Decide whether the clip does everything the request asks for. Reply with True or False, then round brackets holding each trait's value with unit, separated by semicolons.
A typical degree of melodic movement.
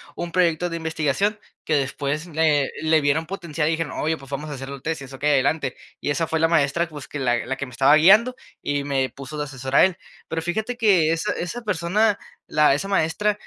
True (3.4 semitones)